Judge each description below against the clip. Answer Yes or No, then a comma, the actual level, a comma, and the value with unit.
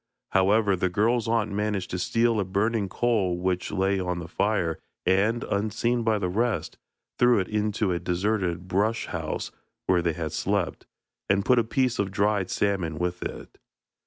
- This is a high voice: No, low, 100 Hz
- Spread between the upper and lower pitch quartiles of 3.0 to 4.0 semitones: Yes, average, 3.4 semitones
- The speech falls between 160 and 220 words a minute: Yes, average, 170 wpm